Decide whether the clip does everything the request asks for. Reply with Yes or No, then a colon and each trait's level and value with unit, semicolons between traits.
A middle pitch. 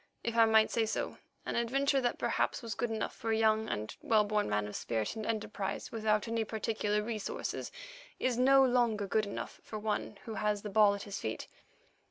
No: high, 220 Hz